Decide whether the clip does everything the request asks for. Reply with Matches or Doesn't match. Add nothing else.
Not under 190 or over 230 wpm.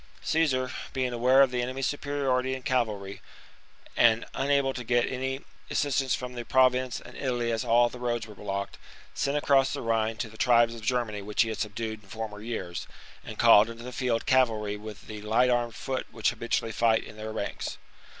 Matches